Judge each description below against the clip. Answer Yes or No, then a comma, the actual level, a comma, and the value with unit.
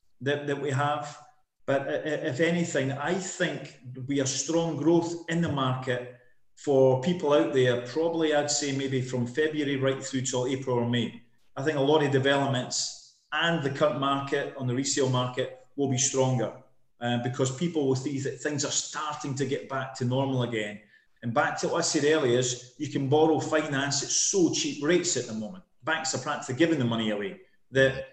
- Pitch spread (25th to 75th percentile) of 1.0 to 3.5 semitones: Yes, average, 3.1 semitones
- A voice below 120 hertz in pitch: No, medium, 140 Hz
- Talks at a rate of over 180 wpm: Yes, average, 195 wpm